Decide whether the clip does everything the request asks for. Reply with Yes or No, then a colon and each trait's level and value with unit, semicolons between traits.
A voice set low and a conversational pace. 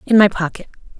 No: high, 190 Hz; average, 180 wpm